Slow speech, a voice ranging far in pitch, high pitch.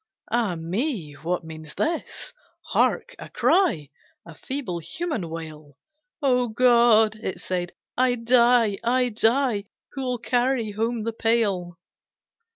Yes: slow, 120 wpm; wide, 6.0 semitones; high, 225 Hz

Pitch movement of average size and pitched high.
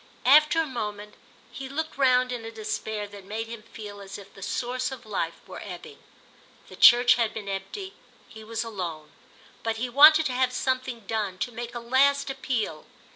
Yes: average, 3.8 semitones; high, 230 Hz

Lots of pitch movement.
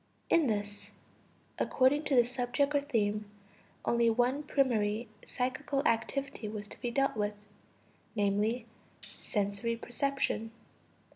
No: average, 4.5 semitones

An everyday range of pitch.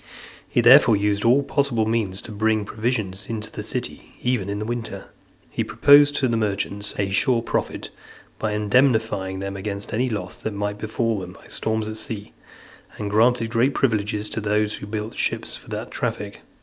No: narrow, 2.3 semitones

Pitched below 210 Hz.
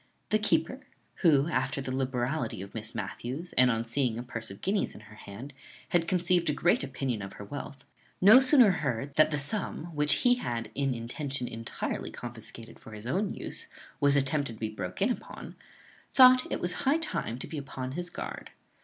Yes: low, 135 Hz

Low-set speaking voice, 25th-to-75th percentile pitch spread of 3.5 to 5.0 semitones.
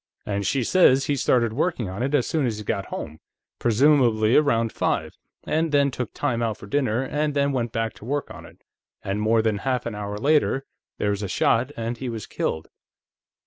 Yes: low, 120 Hz; average, 4.5 semitones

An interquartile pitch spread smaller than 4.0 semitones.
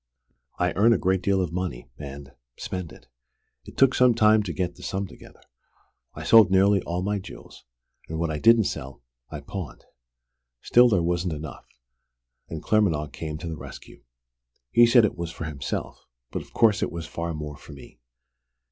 No: average, 4.9 semitones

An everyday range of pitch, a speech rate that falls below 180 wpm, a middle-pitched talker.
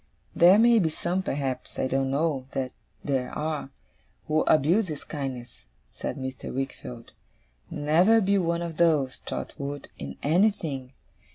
Yes: average, 4.3 semitones; average, 140 wpm; medium, 150 Hz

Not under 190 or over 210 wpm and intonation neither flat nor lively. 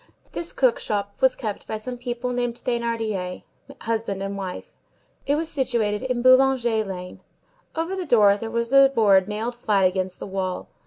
No: average, 170 wpm; average, 4.0 semitones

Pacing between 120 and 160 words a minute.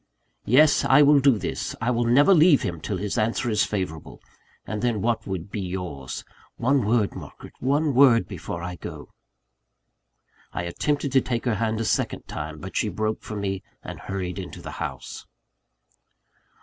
No: average, 175 wpm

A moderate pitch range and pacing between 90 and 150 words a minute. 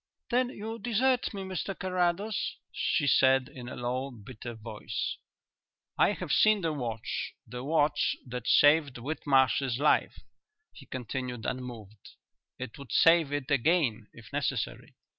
No: wide, 5.8 semitones; slow, 135 wpm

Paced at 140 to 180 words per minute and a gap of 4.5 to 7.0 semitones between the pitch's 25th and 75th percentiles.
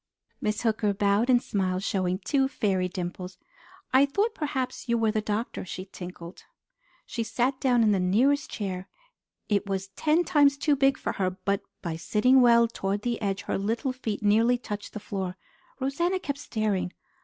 Yes: average, 175 wpm; average, 5.0 semitones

